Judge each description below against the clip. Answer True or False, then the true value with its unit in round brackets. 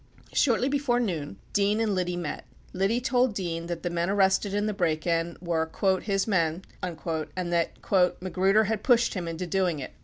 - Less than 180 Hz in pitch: False (185 Hz)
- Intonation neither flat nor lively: True (3.6 semitones)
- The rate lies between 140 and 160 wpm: False (180 wpm)